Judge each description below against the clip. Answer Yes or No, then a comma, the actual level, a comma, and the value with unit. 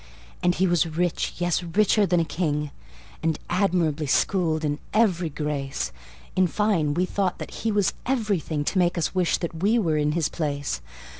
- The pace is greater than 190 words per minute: No, average, 175 wpm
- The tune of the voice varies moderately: Yes, average, 3.5 semitones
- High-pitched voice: No, medium, 170 Hz